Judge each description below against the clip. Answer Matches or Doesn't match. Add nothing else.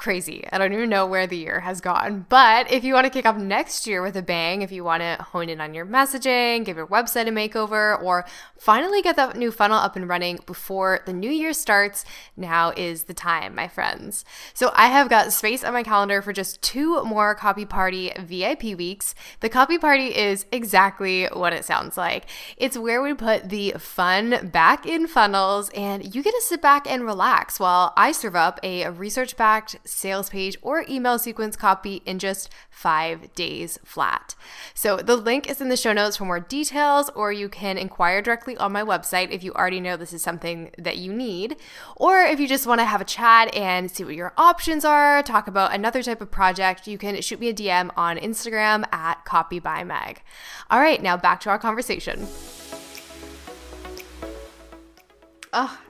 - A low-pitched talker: Doesn't match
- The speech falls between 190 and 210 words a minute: Matches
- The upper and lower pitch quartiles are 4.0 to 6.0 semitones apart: Matches